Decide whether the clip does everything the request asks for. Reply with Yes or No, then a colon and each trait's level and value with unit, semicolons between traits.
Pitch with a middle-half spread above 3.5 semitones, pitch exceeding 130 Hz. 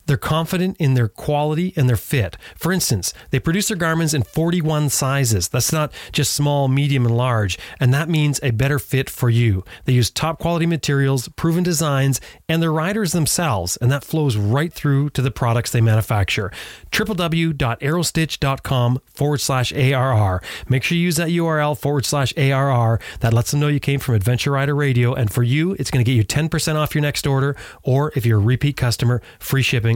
Yes: average, 4.2 semitones; medium, 140 Hz